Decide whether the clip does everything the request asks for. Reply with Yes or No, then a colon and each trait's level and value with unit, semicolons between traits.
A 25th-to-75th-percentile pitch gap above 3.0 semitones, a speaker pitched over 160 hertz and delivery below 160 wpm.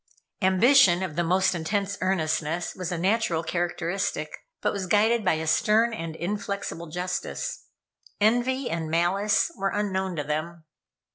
Yes: average, 3.6 semitones; medium, 185 Hz; average, 140 wpm